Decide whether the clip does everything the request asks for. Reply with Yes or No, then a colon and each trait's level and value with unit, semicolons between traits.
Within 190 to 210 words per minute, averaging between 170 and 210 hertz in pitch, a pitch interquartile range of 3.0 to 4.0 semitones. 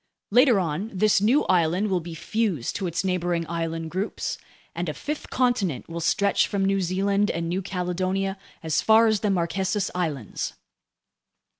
No: average, 160 wpm; medium, 185 Hz; average, 3.3 semitones